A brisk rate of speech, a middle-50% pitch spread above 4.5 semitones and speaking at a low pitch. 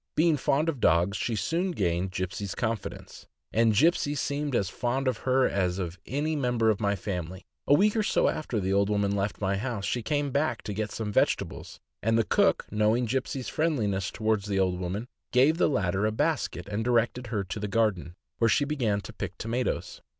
Yes: fast, 210 wpm; average, 5.1 semitones; low, 110 Hz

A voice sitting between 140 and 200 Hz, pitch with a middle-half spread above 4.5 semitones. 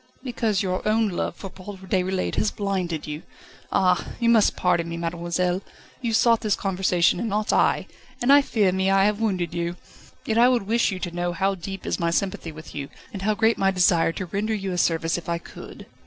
No: high, 190 Hz; average, 3.5 semitones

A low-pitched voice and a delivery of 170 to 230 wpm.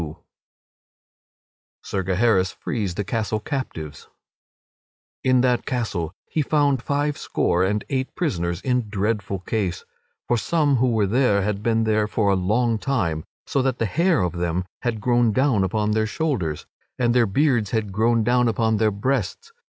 No: low, 110 Hz; average, 160 wpm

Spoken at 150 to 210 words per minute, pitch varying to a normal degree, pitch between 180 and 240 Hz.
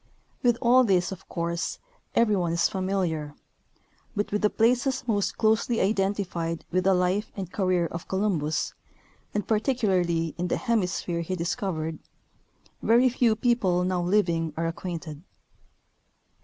No: average, 140 wpm; average, 4.2 semitones; medium, 185 Hz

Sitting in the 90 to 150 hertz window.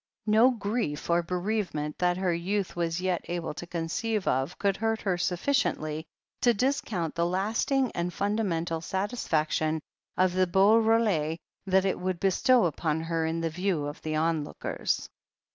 No: medium, 180 Hz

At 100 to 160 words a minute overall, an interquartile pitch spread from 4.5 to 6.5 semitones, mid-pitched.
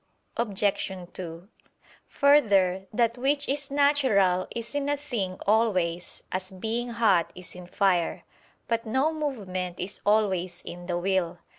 No: slow, 135 wpm; average, 5.0 semitones; high, 200 Hz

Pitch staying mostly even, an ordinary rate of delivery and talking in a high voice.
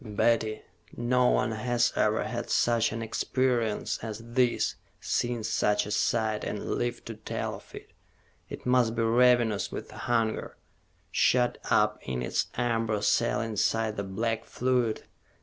No: narrow, 1.9 semitones; average, 145 wpm; low, 115 Hz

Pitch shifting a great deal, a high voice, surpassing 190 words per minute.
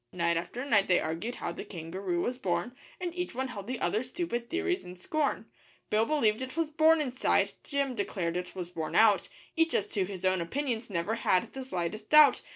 Yes: wide, 7.5 semitones; high, 225 Hz; fast, 205 wpm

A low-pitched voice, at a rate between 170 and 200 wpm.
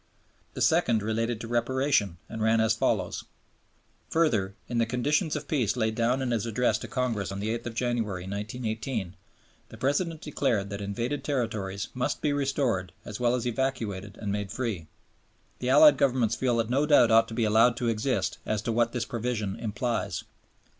Yes: low, 115 Hz; average, 180 wpm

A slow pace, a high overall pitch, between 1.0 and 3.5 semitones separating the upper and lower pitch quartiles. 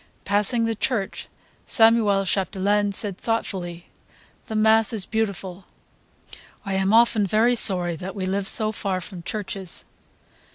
Yes: slow, 130 wpm; high, 200 Hz; narrow, 2.6 semitones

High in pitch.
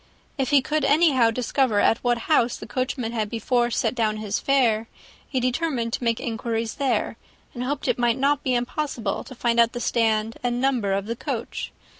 Yes: high, 240 Hz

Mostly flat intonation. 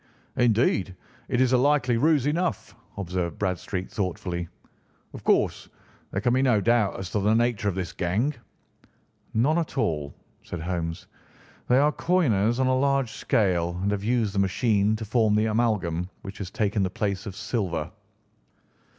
No: average, 4.7 semitones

